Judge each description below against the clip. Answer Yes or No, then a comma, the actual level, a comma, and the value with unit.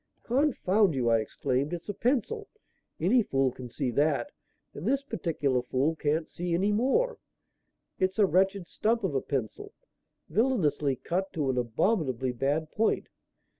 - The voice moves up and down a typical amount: No, wide, 7.9 semitones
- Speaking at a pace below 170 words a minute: Yes, average, 150 wpm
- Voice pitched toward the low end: No, medium, 165 Hz